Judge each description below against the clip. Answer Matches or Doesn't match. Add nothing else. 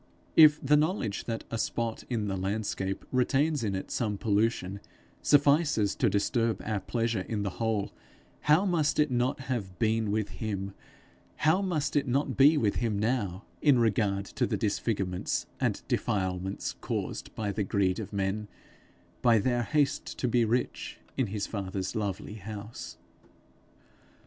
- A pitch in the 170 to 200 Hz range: Doesn't match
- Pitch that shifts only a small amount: Doesn't match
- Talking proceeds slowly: Doesn't match